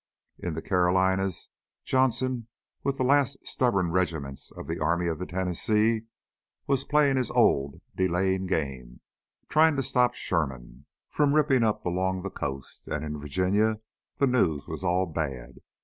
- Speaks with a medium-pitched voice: No, very low, 95 Hz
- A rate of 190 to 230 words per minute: No, average, 150 wpm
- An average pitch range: No, wide, 7.4 semitones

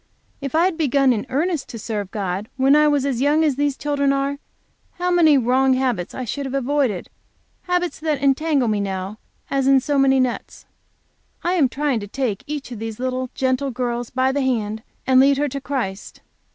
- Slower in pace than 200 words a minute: No, fast, 205 wpm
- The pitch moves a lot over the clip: No, average, 3.0 semitones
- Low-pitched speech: No, very high, 270 Hz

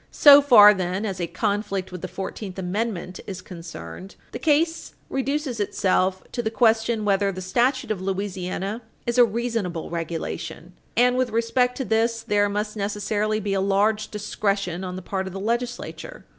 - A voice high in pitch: Yes, high, 205 Hz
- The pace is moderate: Yes, average, 170 wpm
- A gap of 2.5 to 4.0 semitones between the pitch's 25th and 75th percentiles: Yes, average, 3.6 semitones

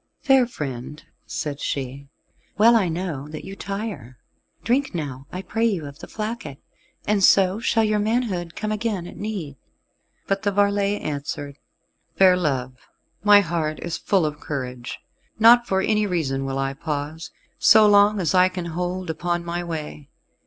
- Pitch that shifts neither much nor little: No, wide, 5.8 semitones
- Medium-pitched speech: Yes, medium, 180 Hz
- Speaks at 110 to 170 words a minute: Yes, average, 160 wpm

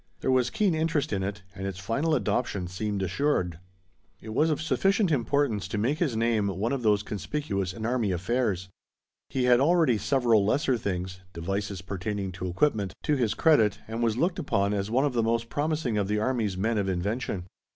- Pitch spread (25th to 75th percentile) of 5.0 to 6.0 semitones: Yes, wide, 5.5 semitones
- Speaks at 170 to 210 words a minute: Yes, average, 195 wpm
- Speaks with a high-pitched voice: No, low, 110 Hz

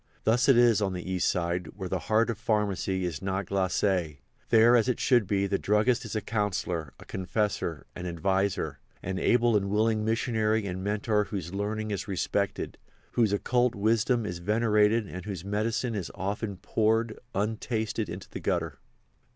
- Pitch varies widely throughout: No, average, 2.9 semitones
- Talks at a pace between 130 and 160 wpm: No, average, 170 wpm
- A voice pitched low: Yes, low, 105 Hz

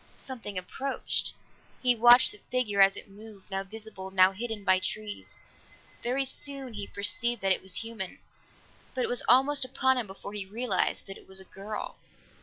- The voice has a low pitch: No, high, 215 Hz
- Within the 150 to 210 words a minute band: Yes, average, 180 wpm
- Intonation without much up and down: No, average, 4.2 semitones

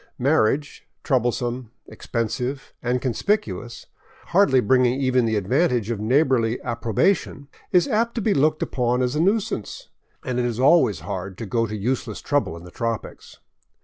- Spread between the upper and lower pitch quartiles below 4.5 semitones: Yes, average, 3.9 semitones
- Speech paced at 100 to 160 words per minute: Yes, average, 150 wpm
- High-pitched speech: No, low, 125 Hz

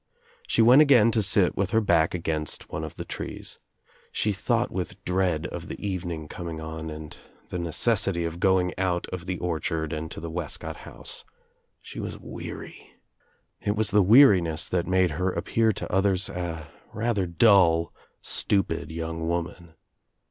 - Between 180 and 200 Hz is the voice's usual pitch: No, very low, 90 Hz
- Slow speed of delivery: No, average, 165 wpm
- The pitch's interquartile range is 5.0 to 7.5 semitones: No, average, 3.2 semitones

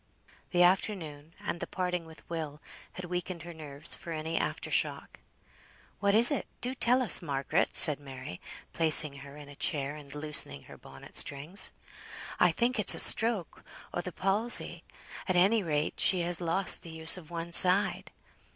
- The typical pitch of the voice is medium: Yes, medium, 170 Hz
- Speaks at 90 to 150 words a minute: No, average, 170 wpm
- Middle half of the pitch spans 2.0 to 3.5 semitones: No, average, 3.9 semitones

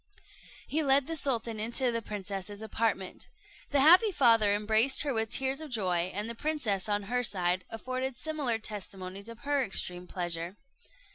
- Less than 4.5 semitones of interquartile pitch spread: No, average, 5.1 semitones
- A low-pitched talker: No, high, 225 Hz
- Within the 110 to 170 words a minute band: Yes, average, 160 wpm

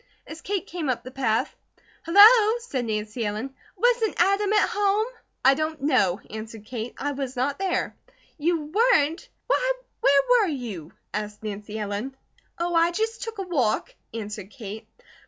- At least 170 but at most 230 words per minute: No, average, 155 wpm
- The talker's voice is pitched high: Yes, very high, 280 Hz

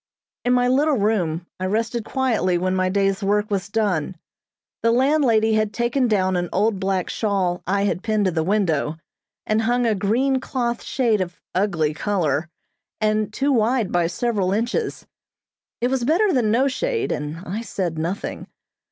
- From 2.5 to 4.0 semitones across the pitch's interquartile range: No, average, 4.5 semitones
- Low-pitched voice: No, high, 210 Hz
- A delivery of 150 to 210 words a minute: Yes, average, 170 wpm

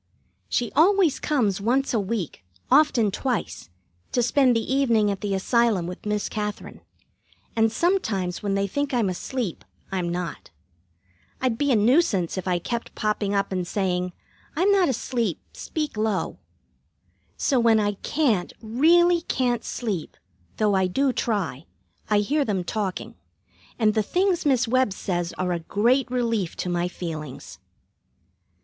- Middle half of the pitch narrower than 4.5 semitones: No, wide, 5.4 semitones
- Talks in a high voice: Yes, high, 220 Hz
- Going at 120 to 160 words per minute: Yes, average, 150 wpm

